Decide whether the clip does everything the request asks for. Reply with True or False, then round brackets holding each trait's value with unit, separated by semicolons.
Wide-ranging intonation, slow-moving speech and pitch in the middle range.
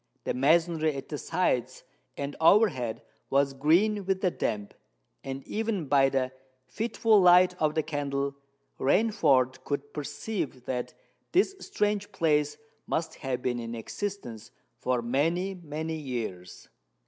True (5.8 semitones; 125 wpm; 150 Hz)